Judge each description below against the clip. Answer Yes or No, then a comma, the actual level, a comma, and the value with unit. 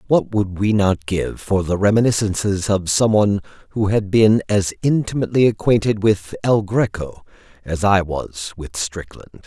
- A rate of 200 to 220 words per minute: No, average, 150 wpm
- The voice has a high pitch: No, low, 100 Hz